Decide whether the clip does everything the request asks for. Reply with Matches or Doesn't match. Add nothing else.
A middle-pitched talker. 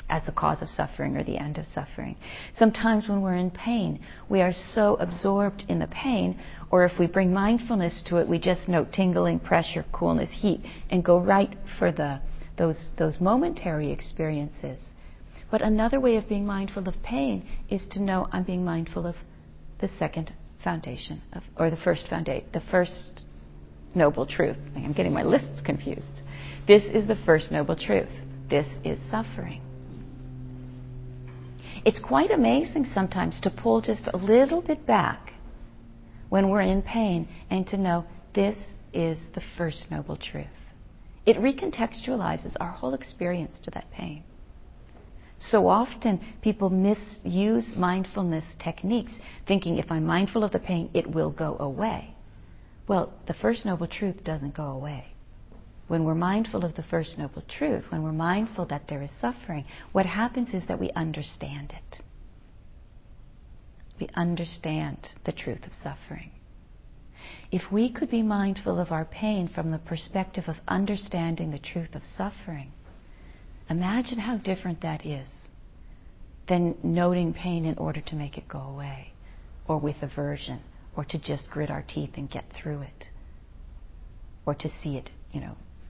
Matches